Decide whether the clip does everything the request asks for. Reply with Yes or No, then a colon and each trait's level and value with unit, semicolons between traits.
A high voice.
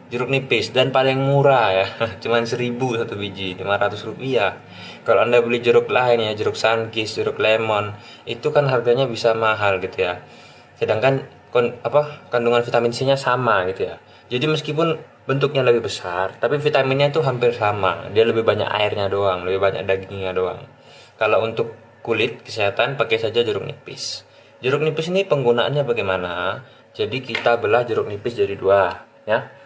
No: low, 120 Hz